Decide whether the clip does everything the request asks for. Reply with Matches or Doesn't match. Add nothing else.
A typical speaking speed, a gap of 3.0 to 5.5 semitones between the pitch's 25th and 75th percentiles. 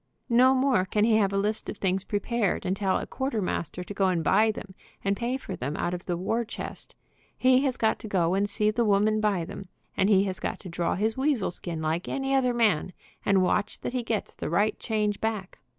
Doesn't match